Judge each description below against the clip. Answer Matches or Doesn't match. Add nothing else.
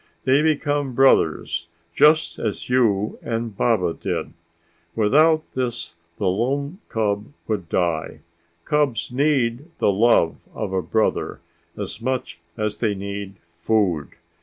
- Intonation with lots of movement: Doesn't match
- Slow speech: Matches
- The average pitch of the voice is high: Doesn't match